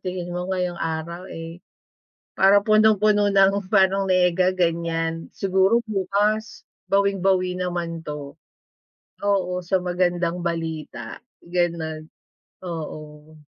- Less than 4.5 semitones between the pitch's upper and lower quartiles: Yes, average, 2.7 semitones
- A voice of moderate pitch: Yes, medium, 180 Hz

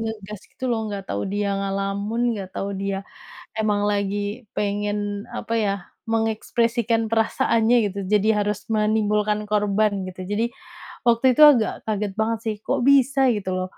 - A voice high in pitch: Yes, high, 210 Hz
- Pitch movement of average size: No, narrow, 1.9 semitones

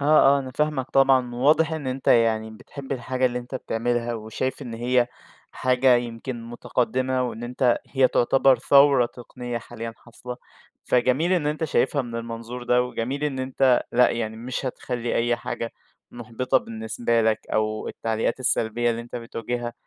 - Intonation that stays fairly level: Yes, narrow, 2.0 semitones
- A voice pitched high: No, low, 125 Hz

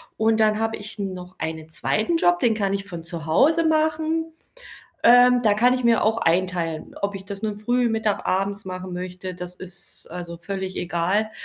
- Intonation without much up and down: No, average, 3.9 semitones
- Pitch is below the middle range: No, high, 200 Hz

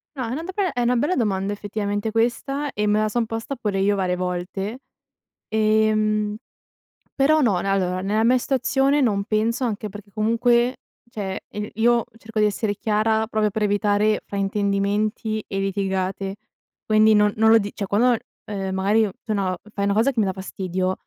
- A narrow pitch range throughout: Yes, narrow, 2.2 semitones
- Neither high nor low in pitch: No, high, 215 Hz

